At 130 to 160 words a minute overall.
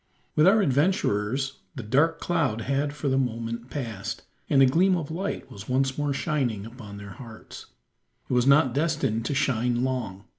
No: average, 175 wpm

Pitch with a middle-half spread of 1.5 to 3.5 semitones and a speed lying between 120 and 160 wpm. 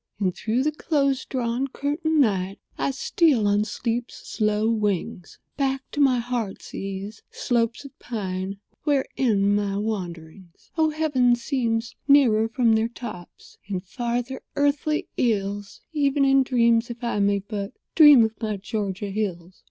No: average, 4.8 semitones; average, 145 wpm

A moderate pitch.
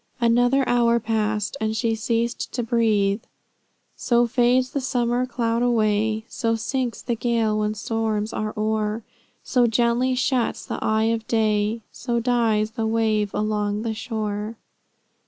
No: high, 225 Hz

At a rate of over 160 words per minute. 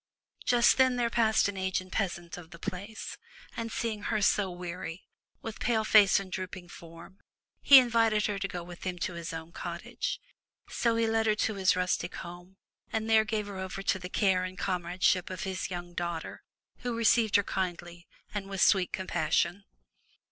Yes: average, 185 wpm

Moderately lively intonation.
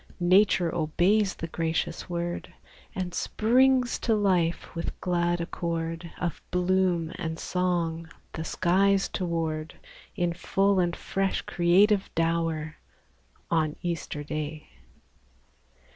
No: narrow, 2.3 semitones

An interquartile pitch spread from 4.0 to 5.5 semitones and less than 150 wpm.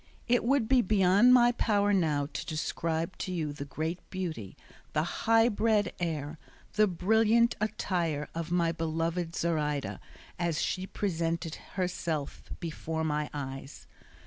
Yes: average, 4.6 semitones; slow, 135 wpm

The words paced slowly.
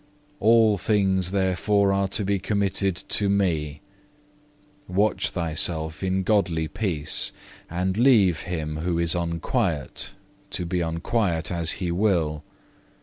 Yes: slow, 125 wpm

